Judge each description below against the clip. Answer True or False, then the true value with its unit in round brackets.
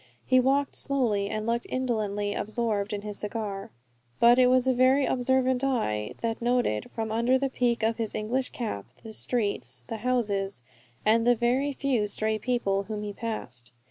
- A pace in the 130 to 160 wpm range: False (175 wpm)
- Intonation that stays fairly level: False (3.4 semitones)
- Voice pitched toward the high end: True (230 Hz)